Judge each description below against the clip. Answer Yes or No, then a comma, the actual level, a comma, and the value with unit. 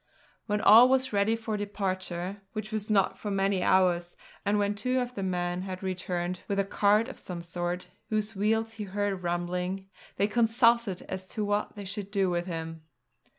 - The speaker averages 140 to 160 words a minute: No, average, 185 wpm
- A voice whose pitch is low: No, high, 200 Hz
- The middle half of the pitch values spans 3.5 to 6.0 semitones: No, average, 2.7 semitones